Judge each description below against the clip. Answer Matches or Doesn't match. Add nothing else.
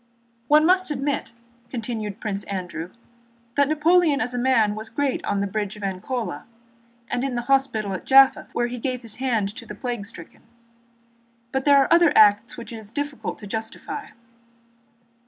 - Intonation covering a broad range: Doesn't match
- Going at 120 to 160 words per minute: Doesn't match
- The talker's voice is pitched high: Matches